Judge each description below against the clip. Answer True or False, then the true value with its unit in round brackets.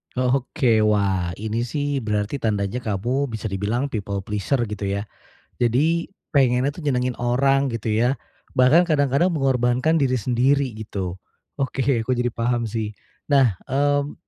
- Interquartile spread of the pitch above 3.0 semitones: True (4.2 semitones)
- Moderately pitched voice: False (125 Hz)